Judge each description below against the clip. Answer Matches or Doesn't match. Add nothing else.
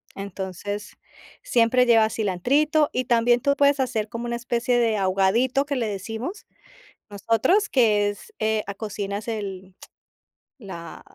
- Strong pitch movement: Doesn't match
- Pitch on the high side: Matches